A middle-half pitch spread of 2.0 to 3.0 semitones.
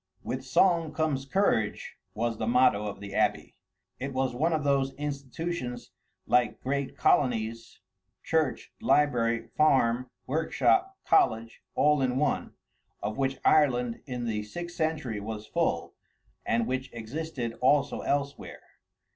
No: average, 4.2 semitones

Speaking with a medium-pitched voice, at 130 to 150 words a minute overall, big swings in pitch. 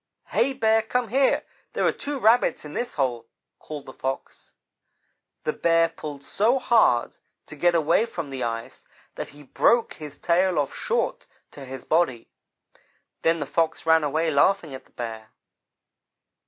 No: medium, 160 Hz; average, 160 wpm; wide, 8.1 semitones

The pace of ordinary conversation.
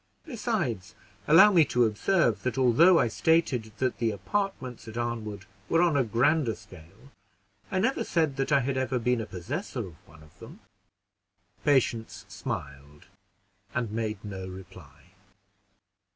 Yes: average, 145 wpm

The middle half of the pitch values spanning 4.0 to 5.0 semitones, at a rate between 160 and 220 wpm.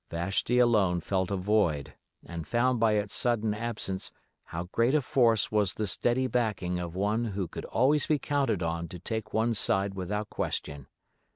Yes: average, 4.4 semitones; average, 175 wpm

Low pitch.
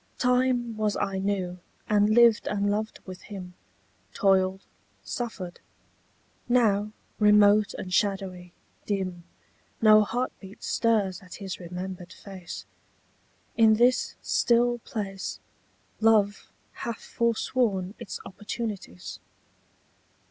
No: high, 205 Hz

